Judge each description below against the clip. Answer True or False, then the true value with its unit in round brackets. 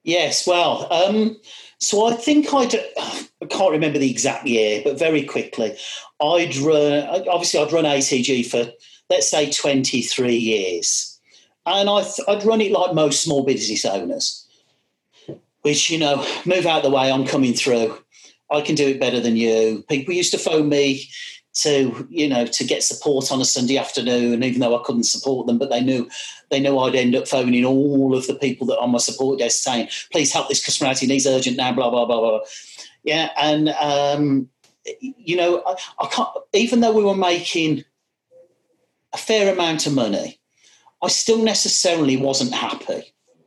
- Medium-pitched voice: True (145 Hz)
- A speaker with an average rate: True (180 wpm)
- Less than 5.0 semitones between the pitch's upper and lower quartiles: False (5.3 semitones)